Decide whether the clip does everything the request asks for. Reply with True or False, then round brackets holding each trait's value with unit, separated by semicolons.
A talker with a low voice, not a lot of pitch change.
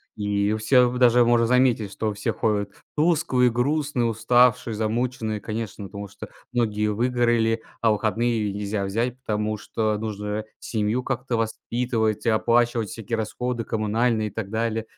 True (115 Hz; 2.3 semitones)